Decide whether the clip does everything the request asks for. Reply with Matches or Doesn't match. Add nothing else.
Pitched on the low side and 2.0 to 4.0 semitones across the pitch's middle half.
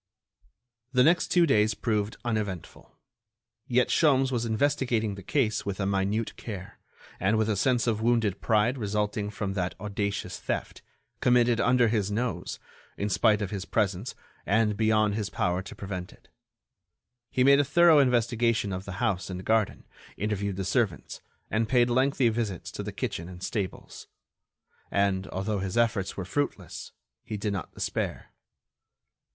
Matches